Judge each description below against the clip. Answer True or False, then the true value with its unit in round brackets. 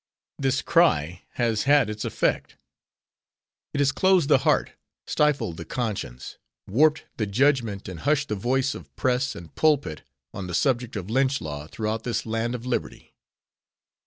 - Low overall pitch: True (120 Hz)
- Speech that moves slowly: False (155 wpm)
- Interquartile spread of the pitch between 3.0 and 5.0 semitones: False (5.6 semitones)